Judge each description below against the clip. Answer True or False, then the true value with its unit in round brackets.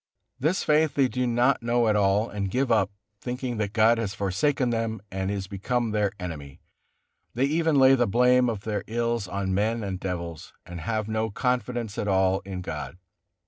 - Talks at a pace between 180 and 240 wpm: True (185 wpm)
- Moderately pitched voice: False (110 Hz)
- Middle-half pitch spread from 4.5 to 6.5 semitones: False (4.1 semitones)